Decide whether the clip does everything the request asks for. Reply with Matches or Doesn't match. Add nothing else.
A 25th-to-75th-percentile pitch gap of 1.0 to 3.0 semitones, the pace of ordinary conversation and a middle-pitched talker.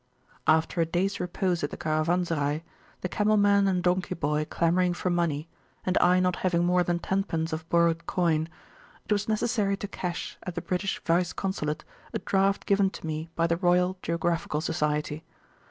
Matches